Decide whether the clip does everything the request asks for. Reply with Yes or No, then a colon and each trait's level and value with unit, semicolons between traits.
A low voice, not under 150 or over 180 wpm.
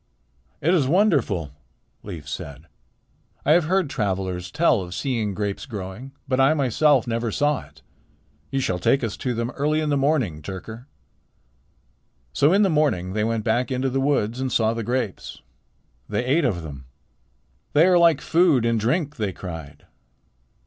Yes: low, 120 Hz; average, 165 wpm